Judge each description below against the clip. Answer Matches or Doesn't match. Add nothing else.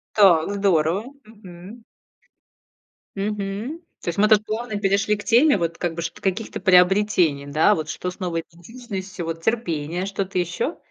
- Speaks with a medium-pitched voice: Doesn't match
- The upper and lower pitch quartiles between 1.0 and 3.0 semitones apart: Doesn't match